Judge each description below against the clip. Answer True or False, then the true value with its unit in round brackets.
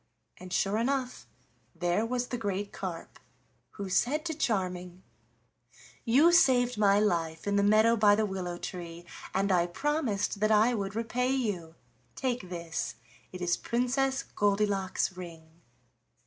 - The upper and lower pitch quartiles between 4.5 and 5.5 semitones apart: True (5.1 semitones)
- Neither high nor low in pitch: False (205 Hz)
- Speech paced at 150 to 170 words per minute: False (140 wpm)